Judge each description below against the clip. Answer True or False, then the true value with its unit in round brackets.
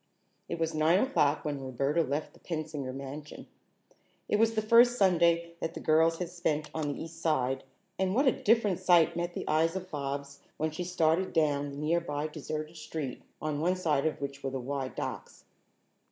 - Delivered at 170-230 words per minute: True (190 wpm)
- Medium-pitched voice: True (160 Hz)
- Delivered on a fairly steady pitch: False (3.1 semitones)